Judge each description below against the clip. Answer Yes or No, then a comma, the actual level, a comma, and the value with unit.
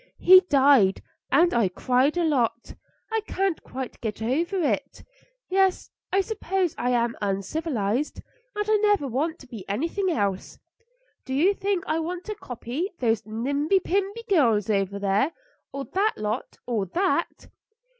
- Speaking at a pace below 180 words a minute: Yes, average, 150 wpm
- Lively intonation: Yes, wide, 8.4 semitones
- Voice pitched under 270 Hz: No, very high, 285 Hz